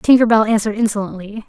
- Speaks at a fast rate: No, average, 160 wpm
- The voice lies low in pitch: No, high, 215 Hz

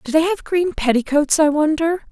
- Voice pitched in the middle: No, very high, 310 Hz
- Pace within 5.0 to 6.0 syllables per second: Yes, 5.2 syllables/s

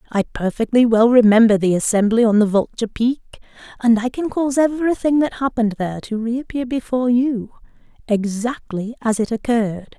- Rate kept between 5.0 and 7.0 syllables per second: Yes, 5.5 syllables/s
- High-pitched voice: Yes, high, 230 Hz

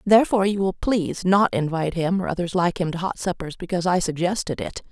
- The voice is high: No, medium, 180 Hz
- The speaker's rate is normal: No, fast, 220 wpm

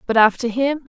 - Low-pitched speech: No, high, 245 Hz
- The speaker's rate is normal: Yes, average, 190 wpm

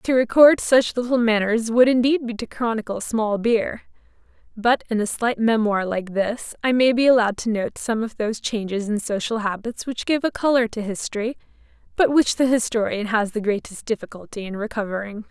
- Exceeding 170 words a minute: Yes, average, 190 wpm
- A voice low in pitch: No, high, 225 Hz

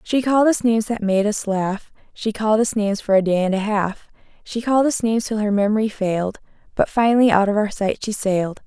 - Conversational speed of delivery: No, fast, 235 wpm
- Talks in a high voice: Yes, high, 215 Hz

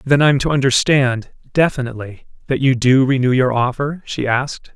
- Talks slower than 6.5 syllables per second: Yes, 5.2 syllables/s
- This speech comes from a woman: No, male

